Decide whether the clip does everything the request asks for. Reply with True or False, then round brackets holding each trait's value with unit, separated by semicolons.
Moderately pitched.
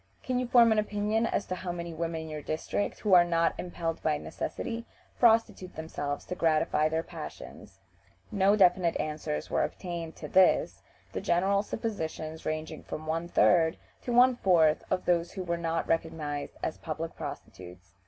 True (170 Hz)